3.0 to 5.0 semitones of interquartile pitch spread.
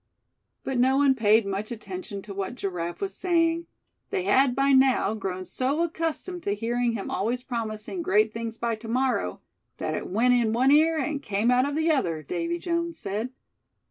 No: wide, 5.6 semitones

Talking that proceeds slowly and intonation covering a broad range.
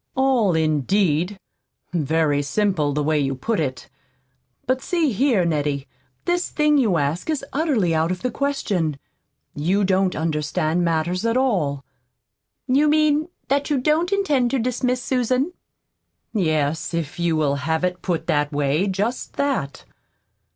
No: average, 145 wpm; wide, 8.9 semitones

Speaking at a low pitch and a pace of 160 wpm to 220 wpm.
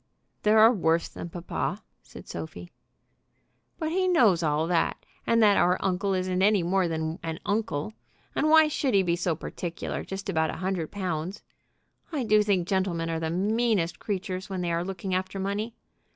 No: medium, 185 Hz; average, 180 wpm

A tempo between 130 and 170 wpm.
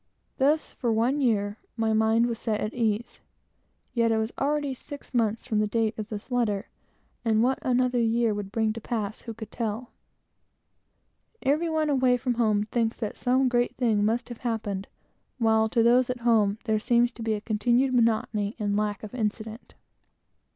No: average, 180 wpm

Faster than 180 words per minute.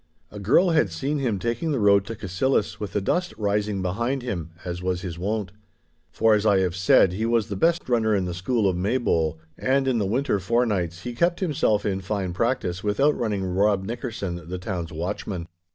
Yes: average, 200 wpm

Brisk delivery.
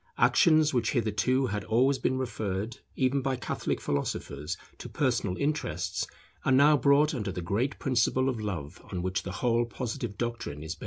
No: average, 170 wpm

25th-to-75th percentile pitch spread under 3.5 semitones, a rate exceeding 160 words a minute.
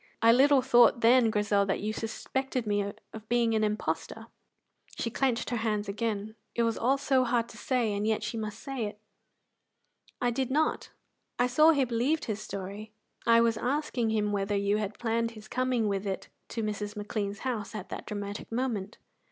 Yes: average, 2.9 semitones; average, 185 wpm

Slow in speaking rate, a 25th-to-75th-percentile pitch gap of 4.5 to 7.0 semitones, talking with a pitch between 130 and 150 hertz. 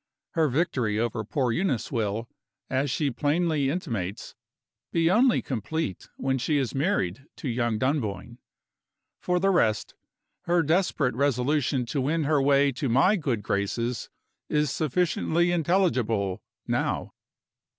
Yes: slow, 130 wpm; wide, 5.5 semitones; medium, 140 Hz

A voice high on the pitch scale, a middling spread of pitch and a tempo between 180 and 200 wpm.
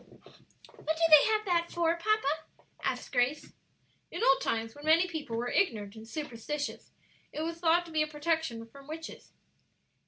No: very high, 310 Hz; average, 4.7 semitones; average, 165 wpm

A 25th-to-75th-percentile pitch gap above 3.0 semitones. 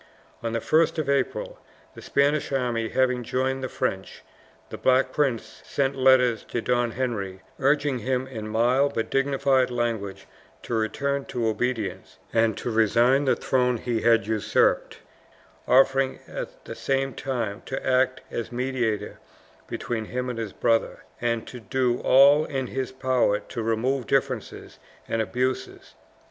No: average, 2.7 semitones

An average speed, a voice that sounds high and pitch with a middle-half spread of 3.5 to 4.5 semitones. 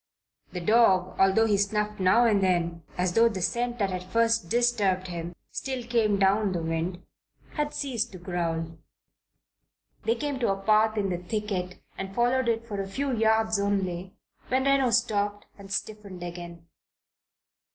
Yes: average, 160 wpm; high, 205 Hz; average, 4.0 semitones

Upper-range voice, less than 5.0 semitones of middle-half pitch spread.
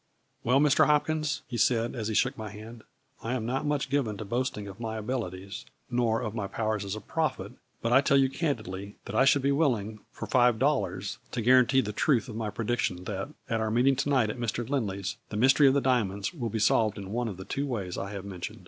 No: low, 115 Hz; average, 4.0 semitones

